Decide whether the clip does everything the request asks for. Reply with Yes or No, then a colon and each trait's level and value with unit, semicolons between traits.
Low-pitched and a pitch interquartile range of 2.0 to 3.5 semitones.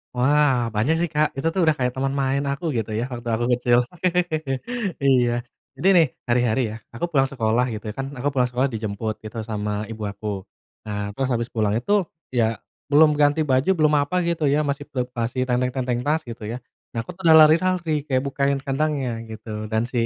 No: low, 130 Hz; average, 3.9 semitones